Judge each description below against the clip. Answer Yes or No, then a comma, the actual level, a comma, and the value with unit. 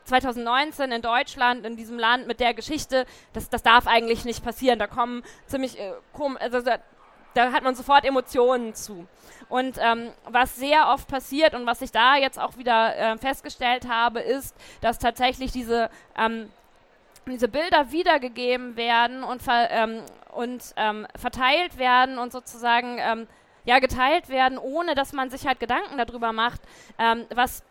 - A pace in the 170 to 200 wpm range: No, average, 160 wpm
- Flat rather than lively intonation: Yes, narrow, 2.0 semitones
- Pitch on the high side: Yes, high, 245 Hz